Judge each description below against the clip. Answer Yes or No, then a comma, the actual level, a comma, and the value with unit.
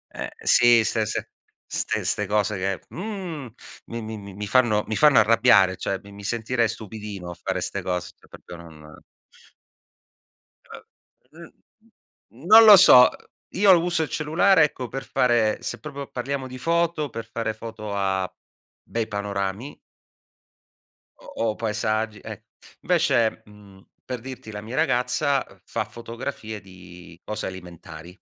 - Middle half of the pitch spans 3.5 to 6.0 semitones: Yes, average, 4.6 semitones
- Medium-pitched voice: No, low, 110 Hz